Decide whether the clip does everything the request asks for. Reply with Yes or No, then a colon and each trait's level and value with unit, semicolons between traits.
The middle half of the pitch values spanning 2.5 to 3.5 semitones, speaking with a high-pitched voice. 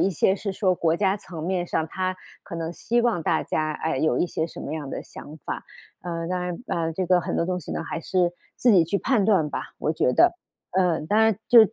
No: average, 3.1 semitones; medium, 180 Hz